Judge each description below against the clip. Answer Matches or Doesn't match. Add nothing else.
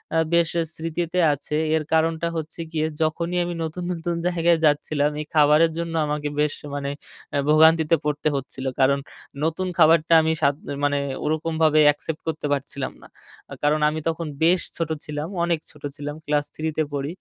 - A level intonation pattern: Matches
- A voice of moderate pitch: Matches